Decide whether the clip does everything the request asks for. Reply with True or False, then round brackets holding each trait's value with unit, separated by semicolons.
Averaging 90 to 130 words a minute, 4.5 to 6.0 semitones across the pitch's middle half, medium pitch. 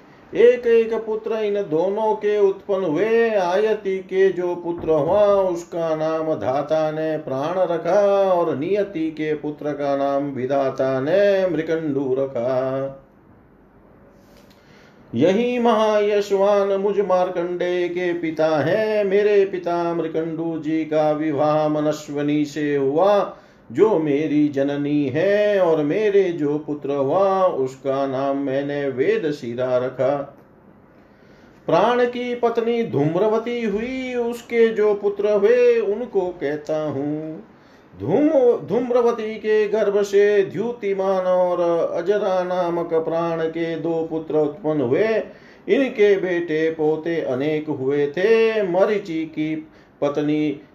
True (115 wpm; 5.2 semitones; 170 Hz)